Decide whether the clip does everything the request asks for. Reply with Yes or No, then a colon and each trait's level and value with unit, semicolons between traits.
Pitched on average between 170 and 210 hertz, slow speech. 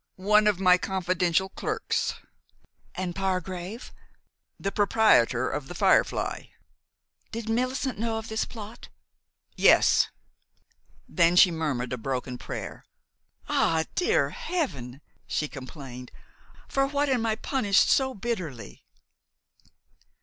Yes: high, 190 Hz; slow, 110 wpm